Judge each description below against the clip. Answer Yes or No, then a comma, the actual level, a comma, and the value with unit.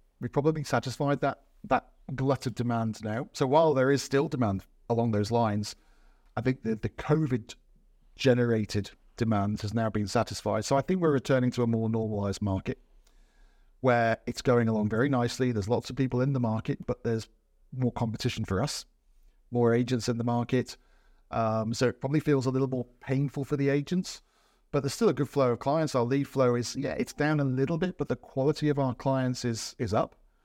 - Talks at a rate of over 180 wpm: Yes, average, 200 wpm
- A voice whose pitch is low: Yes, low, 125 Hz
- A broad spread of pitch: No, average, 3.4 semitones